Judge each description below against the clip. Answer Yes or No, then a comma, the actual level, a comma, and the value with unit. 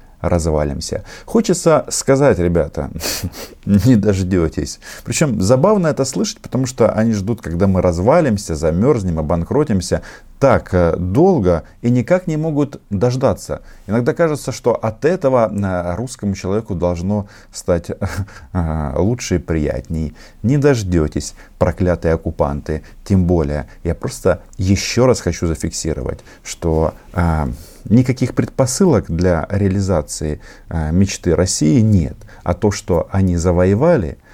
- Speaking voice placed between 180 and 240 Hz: No, very low, 95 Hz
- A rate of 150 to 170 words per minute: No, slow, 110 wpm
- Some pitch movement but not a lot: No, wide, 5.9 semitones